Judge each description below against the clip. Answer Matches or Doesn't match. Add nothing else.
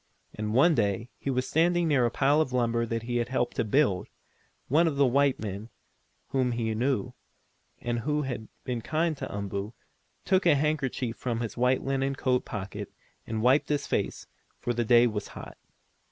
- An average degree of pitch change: Matches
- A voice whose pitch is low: Matches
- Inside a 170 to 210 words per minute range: Matches